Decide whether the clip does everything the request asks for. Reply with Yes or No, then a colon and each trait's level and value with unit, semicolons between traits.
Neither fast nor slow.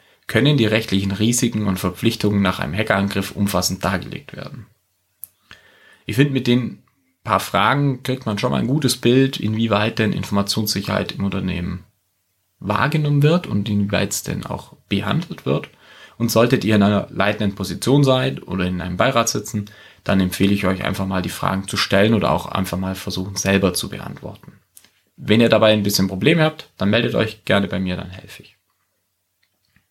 Yes: average, 175 wpm